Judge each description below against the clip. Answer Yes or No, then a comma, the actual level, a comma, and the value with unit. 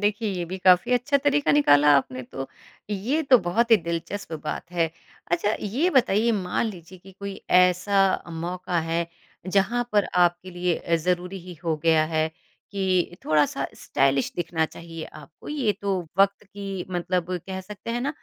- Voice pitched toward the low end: No, medium, 185 Hz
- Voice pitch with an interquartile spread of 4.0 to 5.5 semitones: No, average, 3.4 semitones